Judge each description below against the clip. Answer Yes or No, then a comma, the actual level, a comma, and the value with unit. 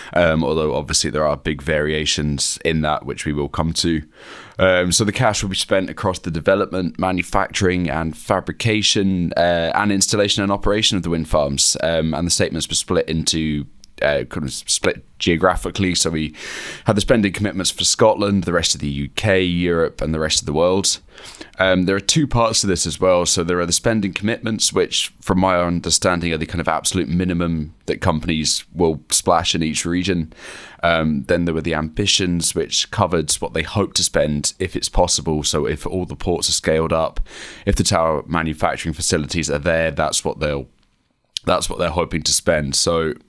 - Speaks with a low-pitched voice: Yes, very low, 85 Hz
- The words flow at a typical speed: Yes, average, 195 wpm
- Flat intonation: No, average, 3.2 semitones